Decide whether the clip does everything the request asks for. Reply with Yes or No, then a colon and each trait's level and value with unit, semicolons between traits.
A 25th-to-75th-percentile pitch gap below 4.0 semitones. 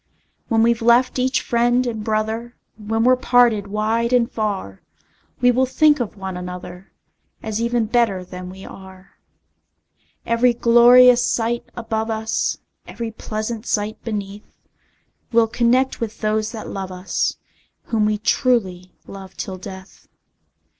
Yes: average, 3.0 semitones